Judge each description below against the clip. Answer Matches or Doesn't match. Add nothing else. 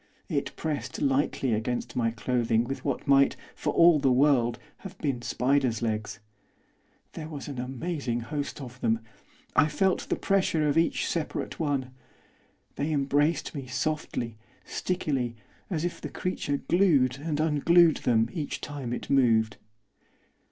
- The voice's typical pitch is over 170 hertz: Doesn't match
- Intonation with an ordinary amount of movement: Matches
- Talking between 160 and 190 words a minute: Doesn't match